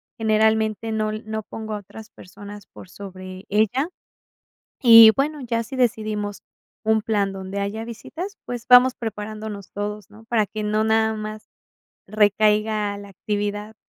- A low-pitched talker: No, high, 215 Hz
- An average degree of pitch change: No, narrow, 1.4 semitones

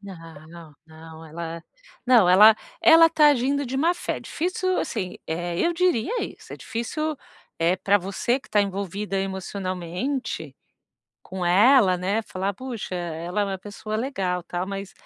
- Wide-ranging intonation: Yes, wide, 6.4 semitones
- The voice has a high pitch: Yes, high, 195 Hz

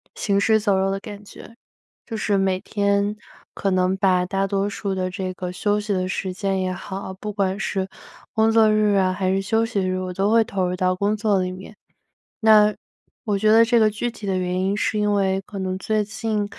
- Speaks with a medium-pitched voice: No, high, 200 Hz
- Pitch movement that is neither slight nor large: No, narrow, 2.1 semitones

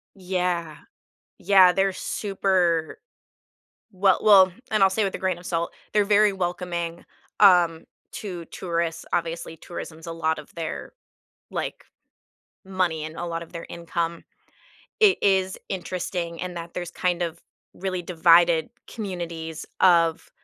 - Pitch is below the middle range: No, medium, 175 Hz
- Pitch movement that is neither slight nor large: No, narrow, 2.1 semitones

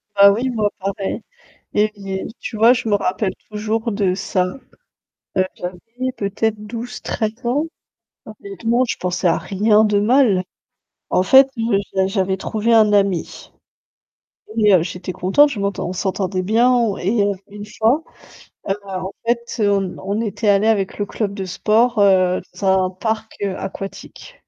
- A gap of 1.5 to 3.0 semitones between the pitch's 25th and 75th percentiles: Yes, average, 2.7 semitones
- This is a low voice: No, high, 205 Hz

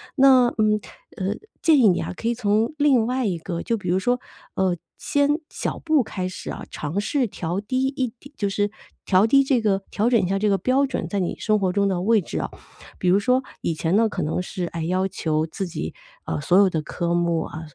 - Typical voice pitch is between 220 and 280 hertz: No, high, 200 Hz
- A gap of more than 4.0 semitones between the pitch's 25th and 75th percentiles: Yes, wide, 5.5 semitones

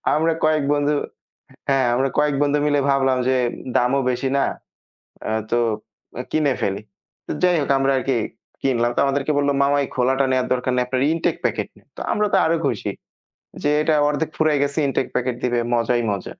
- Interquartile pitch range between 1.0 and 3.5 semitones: Yes, average, 2.7 semitones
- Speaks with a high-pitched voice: No, low, 135 Hz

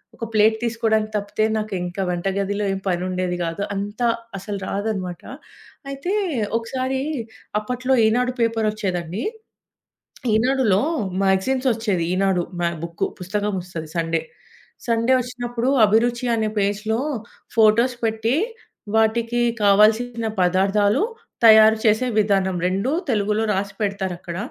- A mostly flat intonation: No, average, 3.1 semitones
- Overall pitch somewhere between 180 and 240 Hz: Yes, high, 215 Hz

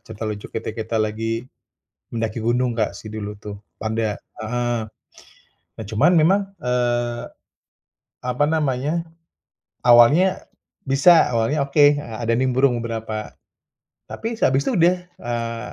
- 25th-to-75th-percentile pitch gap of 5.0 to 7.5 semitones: No, average, 3.7 semitones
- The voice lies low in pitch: Yes, low, 120 Hz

